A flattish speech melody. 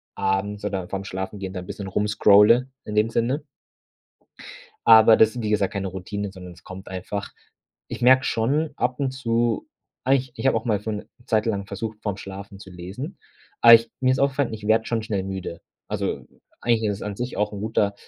No: average, 3.1 semitones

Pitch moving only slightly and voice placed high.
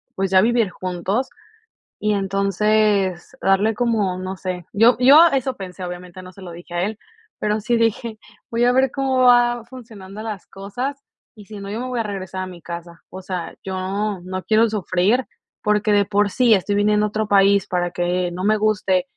No: average, 3.3 semitones; high, 205 Hz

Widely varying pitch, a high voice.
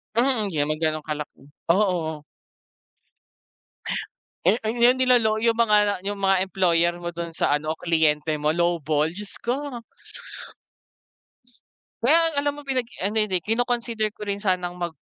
Yes: wide, 6.1 semitones; high, 195 Hz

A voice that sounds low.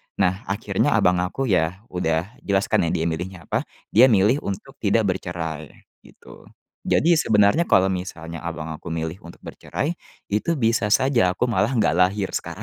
Yes: very low, 95 Hz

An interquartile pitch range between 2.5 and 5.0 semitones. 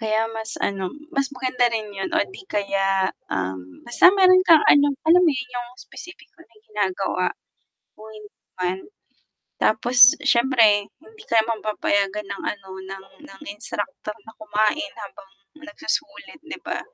No: wide, 5.5 semitones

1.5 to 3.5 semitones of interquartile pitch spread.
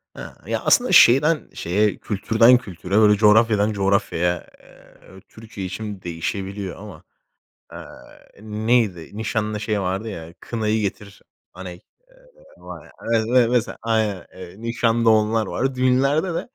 Yes: average, 3.1 semitones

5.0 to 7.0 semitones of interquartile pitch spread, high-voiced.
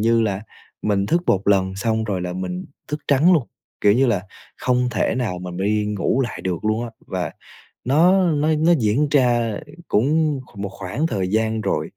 No: average, 5.3 semitones; low, 110 Hz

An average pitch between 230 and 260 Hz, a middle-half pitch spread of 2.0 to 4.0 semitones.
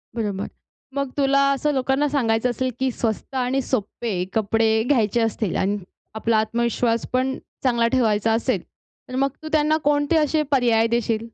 Yes: high, 240 Hz; average, 3.4 semitones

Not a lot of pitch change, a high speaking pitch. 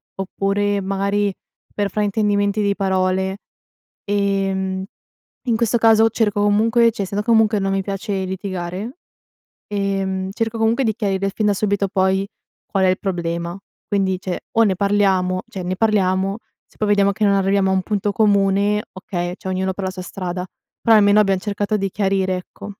Yes: narrow, 1.6 semitones; high, 195 Hz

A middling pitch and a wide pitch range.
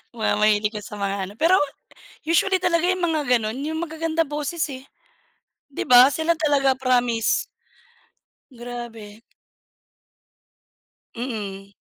No: very high, 260 Hz; wide, 6.5 semitones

